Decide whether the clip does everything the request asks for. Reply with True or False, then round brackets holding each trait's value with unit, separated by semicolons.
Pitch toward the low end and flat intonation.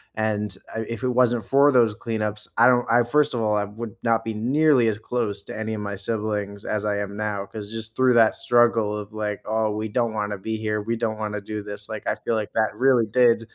True (110 Hz; 1.9 semitones)